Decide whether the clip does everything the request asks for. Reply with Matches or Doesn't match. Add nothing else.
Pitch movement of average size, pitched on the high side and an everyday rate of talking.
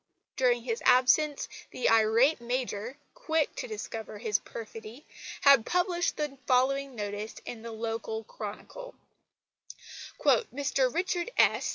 Doesn't match